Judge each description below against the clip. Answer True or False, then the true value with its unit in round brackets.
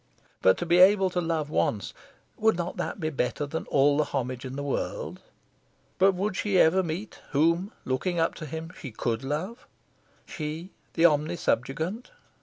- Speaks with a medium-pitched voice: True (160 Hz)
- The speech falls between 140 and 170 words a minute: True (165 wpm)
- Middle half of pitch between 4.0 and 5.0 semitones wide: True (4.3 semitones)